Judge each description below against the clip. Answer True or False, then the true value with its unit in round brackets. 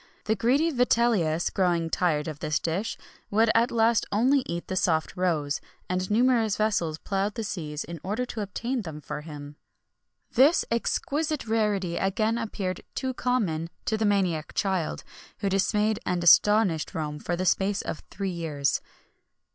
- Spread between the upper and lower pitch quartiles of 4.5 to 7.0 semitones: True (5.2 semitones)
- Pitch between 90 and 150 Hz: False (195 Hz)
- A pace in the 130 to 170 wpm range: True (160 wpm)